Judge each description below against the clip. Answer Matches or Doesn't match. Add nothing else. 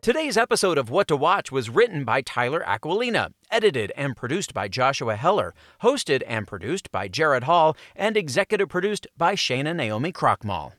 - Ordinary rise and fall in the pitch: Doesn't match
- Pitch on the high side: Matches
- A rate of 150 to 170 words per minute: Matches